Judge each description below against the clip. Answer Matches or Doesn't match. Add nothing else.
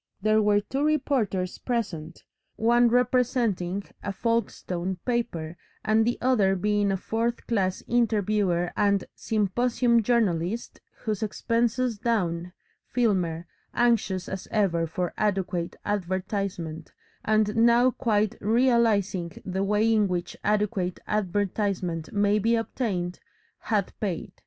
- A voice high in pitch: Matches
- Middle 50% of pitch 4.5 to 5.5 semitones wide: Doesn't match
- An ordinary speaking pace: Doesn't match